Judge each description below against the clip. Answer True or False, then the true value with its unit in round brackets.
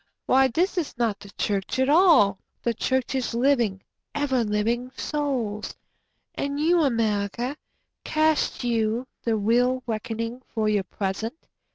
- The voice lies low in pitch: False (240 Hz)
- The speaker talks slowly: True (115 wpm)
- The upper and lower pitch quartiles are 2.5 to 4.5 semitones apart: True (4.0 semitones)